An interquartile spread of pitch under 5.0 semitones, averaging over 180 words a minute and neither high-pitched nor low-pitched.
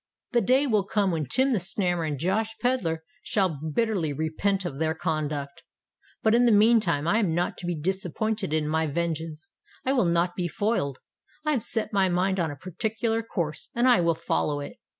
No: wide, 5.5 semitones; average, 190 wpm; medium, 180 Hz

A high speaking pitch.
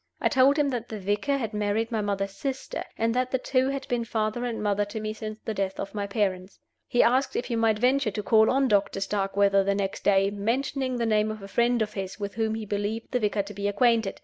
Yes: high, 215 Hz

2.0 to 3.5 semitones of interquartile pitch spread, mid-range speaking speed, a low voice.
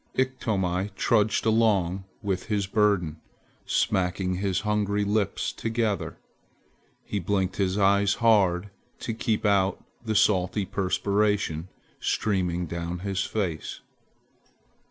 No: narrow, 2.4 semitones; slow, 105 wpm; low, 100 Hz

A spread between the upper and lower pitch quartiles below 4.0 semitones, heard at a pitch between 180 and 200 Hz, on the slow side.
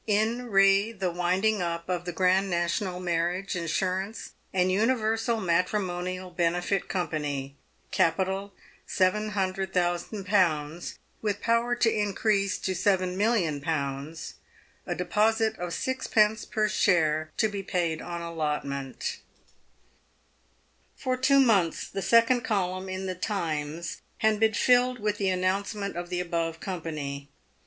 Yes: average, 3.6 semitones; medium, 185 Hz; slow, 115 wpm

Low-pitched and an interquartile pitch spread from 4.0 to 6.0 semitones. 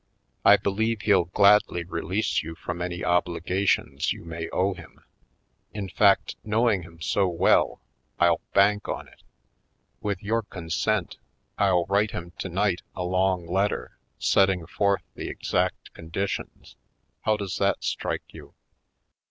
No: very low, 95 Hz; average, 2.7 semitones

